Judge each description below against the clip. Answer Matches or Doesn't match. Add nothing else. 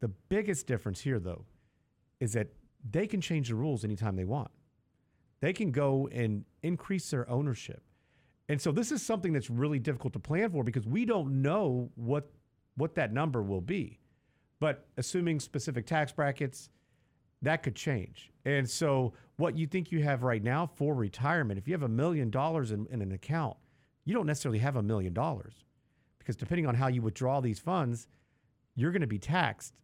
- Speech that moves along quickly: Doesn't match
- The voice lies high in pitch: Doesn't match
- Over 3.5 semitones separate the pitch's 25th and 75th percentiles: Matches